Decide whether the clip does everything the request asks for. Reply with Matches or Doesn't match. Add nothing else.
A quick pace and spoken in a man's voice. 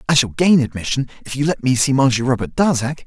Matches